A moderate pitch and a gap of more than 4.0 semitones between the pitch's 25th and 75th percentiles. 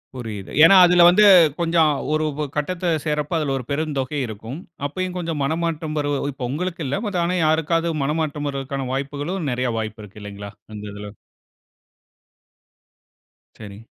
Yes: medium, 150 Hz; average, 4.6 semitones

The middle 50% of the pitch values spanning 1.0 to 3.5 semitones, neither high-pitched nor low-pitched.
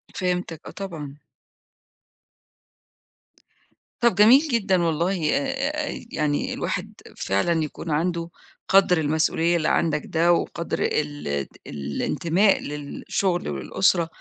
No: average, 4.1 semitones; medium, 170 Hz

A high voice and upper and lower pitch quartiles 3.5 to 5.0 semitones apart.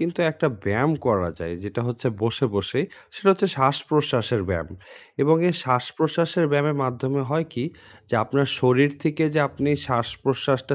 No: low, 135 Hz; average, 4.1 semitones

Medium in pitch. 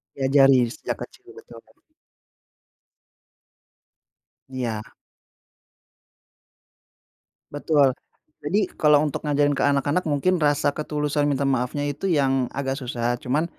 Yes: medium, 145 Hz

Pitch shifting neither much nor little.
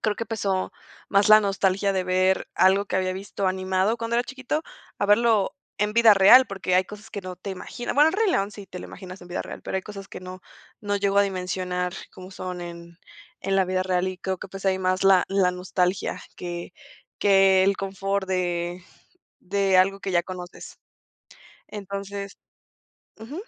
No: narrow, 1.6 semitones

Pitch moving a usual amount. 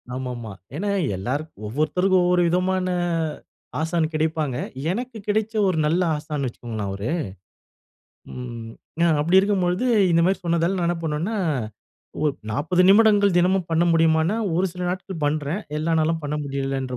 Yes: average, 4.0 semitones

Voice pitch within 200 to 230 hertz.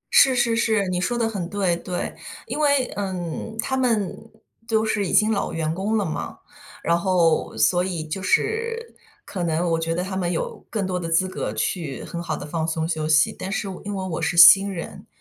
No: medium, 185 Hz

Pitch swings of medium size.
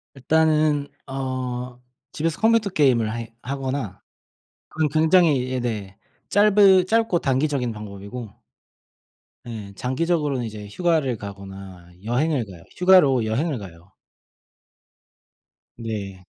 No: wide, 6.5 semitones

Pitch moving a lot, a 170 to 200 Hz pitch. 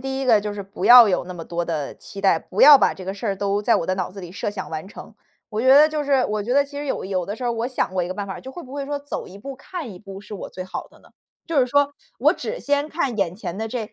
No: wide, 6.0 semitones; high, 215 Hz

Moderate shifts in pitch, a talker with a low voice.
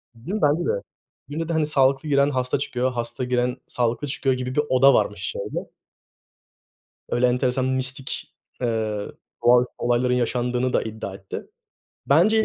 No: narrow, 2.2 semitones; low, 125 Hz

